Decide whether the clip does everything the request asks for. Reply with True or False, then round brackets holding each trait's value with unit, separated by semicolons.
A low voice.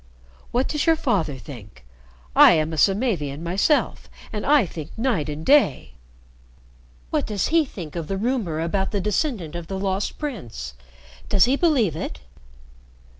False (190 Hz)